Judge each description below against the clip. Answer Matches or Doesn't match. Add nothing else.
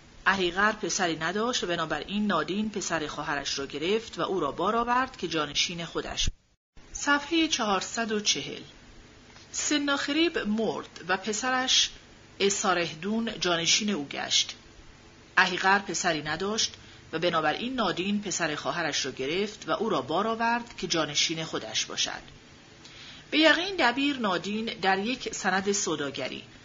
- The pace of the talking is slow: Doesn't match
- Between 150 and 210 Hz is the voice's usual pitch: Matches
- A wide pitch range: Matches